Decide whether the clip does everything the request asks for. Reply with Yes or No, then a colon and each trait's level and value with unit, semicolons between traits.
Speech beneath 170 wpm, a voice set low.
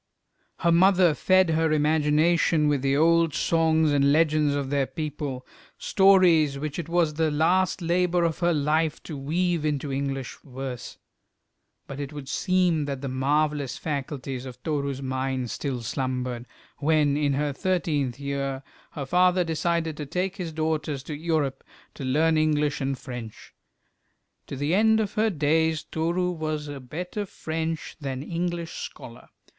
No: average, 150 wpm; medium, 150 Hz